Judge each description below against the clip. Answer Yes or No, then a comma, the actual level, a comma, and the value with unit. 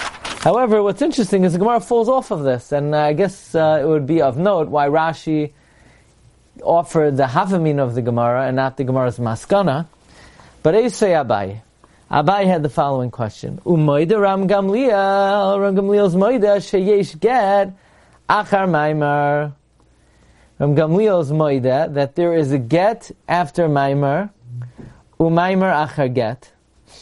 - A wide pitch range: Yes, wide, 6.0 semitones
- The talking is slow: Yes, slow, 130 wpm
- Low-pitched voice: No, medium, 160 Hz